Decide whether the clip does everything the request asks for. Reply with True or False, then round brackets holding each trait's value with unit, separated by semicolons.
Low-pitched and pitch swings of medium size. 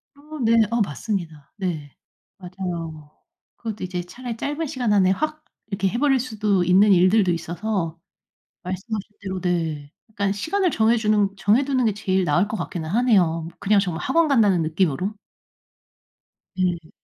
False (195 Hz; 4.4 semitones)